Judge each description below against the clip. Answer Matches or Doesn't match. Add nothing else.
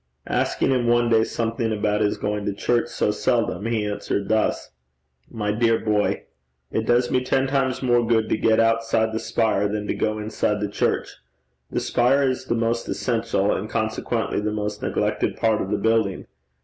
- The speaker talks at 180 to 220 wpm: Matches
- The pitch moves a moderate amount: Doesn't match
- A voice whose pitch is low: Matches